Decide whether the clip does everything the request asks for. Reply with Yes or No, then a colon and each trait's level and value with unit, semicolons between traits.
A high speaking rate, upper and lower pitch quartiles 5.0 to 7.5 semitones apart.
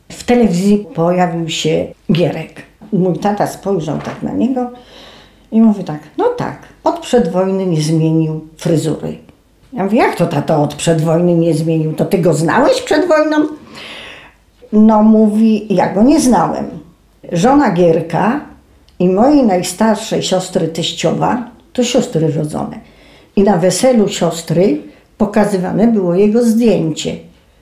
No: average, 130 wpm; wide, 5.6 semitones